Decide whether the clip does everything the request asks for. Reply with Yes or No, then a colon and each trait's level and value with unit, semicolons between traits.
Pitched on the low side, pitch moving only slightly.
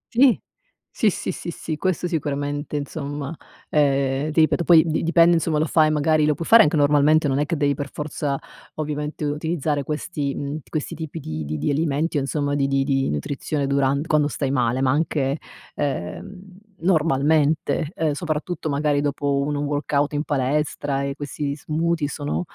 No: medium, 145 Hz; narrow, 2.0 semitones